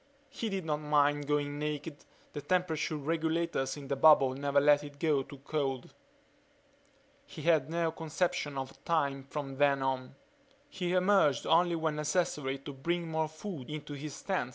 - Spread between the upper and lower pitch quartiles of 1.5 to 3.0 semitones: Yes, narrow, 2.6 semitones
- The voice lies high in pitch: No, medium, 150 Hz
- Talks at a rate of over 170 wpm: No, average, 160 wpm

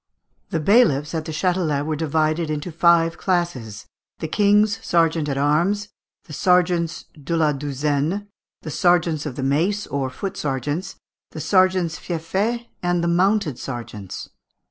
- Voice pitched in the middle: Yes, medium, 165 Hz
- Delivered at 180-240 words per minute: No, average, 145 wpm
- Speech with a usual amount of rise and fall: Yes, average, 3.7 semitones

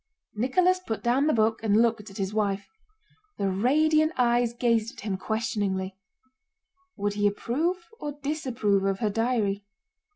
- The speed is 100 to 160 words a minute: Yes, average, 150 wpm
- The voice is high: Yes, high, 225 Hz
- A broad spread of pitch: No, average, 4.3 semitones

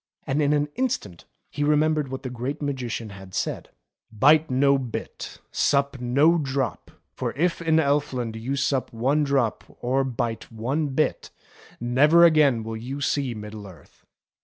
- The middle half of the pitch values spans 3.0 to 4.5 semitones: Yes, average, 3.7 semitones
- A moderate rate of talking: Yes, average, 160 wpm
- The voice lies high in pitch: No, low, 135 Hz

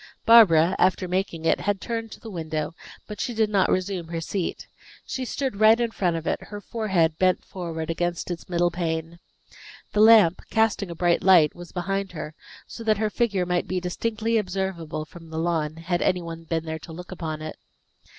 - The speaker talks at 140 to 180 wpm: No, average, 200 wpm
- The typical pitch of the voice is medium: Yes, medium, 180 Hz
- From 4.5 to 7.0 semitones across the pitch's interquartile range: No, average, 3.8 semitones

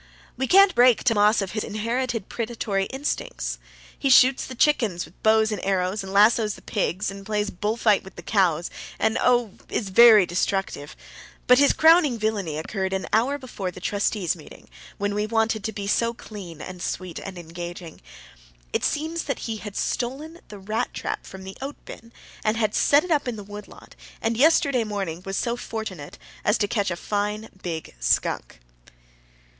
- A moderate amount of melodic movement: Yes, average, 3.8 semitones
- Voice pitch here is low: No, high, 210 Hz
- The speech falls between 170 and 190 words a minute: Yes, average, 180 wpm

